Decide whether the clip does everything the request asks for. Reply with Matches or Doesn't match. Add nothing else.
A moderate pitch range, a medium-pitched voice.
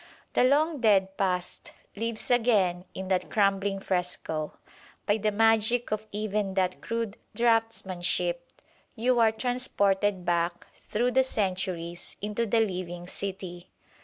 Doesn't match